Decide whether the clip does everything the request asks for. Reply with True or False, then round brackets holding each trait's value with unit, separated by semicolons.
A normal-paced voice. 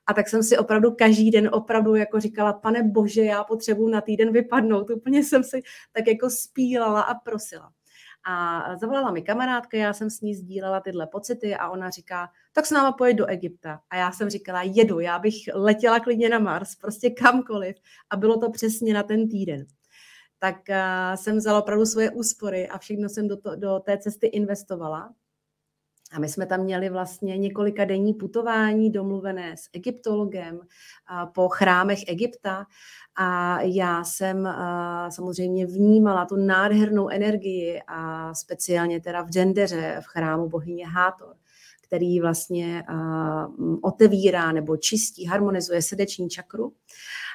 True (150 wpm)